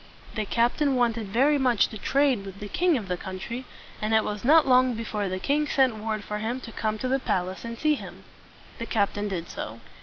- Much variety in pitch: No, average, 4.0 semitones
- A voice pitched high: Yes, high, 230 Hz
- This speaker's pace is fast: Yes, fast, 220 wpm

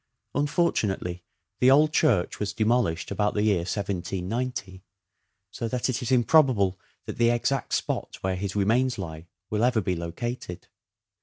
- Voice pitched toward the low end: Yes, low, 105 Hz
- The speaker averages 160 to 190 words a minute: No, average, 150 wpm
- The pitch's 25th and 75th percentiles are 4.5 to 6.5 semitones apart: Yes, average, 5.0 semitones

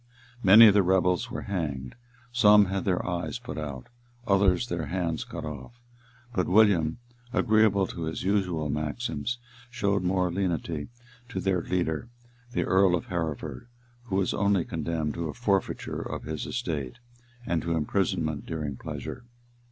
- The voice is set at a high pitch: No, very low, 90 Hz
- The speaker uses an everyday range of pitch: Yes, average, 4.1 semitones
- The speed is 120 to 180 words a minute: Yes, average, 150 wpm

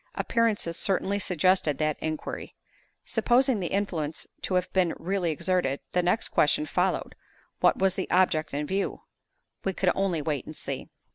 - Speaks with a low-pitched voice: No, medium, 180 Hz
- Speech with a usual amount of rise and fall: Yes, average, 3.7 semitones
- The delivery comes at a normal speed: Yes, average, 155 wpm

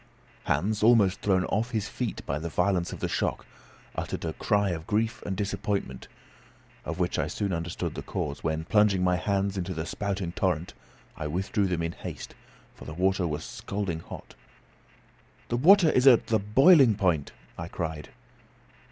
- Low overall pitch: Yes, very low, 95 Hz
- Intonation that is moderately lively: Yes, average, 3.9 semitones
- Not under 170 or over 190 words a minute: Yes, average, 175 wpm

